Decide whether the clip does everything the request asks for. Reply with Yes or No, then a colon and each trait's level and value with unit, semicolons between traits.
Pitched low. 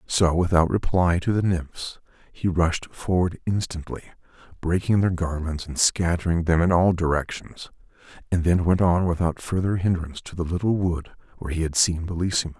Yes: very low, 85 Hz